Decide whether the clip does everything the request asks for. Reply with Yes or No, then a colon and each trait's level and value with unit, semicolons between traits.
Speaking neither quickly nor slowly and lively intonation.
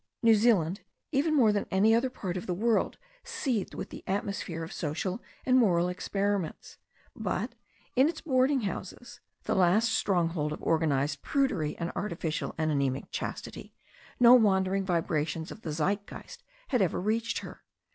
Yes: average, 155 wpm; wide, 5.9 semitones